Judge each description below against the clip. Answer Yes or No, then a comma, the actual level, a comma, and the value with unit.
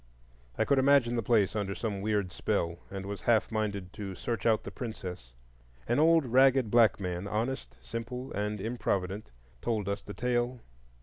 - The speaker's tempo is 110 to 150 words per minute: No, average, 170 wpm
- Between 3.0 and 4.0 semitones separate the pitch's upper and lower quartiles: Yes, average, 3.4 semitones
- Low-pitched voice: Yes, low, 110 Hz